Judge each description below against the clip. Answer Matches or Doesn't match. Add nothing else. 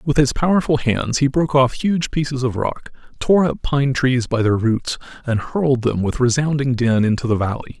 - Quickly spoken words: Matches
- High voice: Doesn't match